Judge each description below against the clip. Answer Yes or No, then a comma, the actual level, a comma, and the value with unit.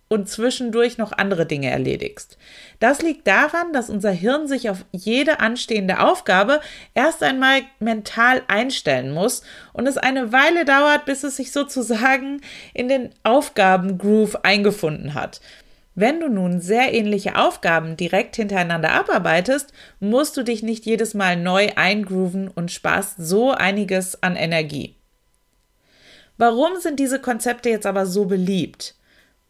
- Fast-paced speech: No, average, 135 wpm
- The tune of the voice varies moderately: No, wide, 5.8 semitones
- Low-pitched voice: No, high, 225 Hz